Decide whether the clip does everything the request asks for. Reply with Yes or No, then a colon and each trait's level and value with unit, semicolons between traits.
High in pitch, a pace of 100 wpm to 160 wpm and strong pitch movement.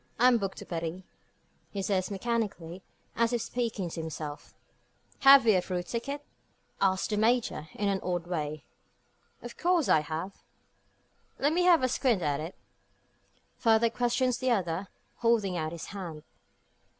Yes: high, 200 Hz; average, 155 wpm; wide, 5.7 semitones